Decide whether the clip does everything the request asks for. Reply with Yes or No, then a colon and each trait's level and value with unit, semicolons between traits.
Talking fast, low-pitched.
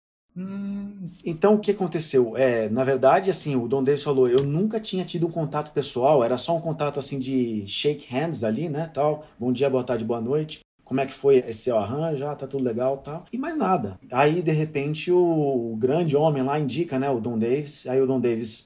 No: fast, 220 wpm; medium, 145 Hz